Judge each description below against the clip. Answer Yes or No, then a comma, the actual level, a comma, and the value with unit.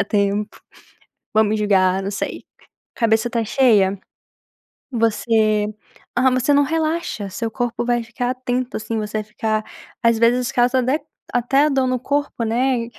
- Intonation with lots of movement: No, average, 3.0 semitones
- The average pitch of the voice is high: Yes, high, 230 Hz